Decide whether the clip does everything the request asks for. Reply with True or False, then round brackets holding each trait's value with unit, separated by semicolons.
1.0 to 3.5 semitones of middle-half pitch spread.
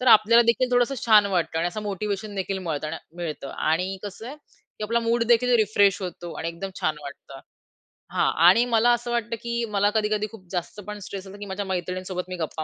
False (4.0 semitones)